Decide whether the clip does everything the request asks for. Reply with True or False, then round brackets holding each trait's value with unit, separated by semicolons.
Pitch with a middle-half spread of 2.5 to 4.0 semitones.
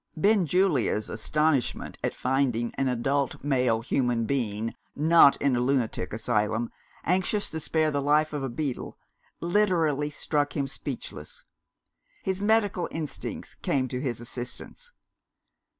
False (4.8 semitones)